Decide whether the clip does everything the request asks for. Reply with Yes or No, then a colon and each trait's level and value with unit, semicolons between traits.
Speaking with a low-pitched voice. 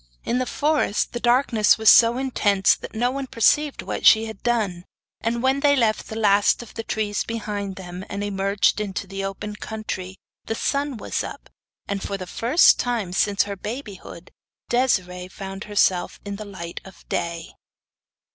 No: high, 210 Hz